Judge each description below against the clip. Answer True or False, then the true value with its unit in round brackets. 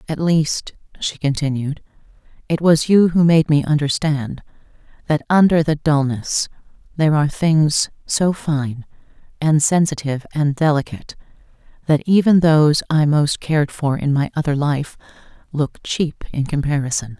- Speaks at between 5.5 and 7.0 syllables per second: False (4.7 syllables/s)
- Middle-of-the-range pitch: True (150 Hz)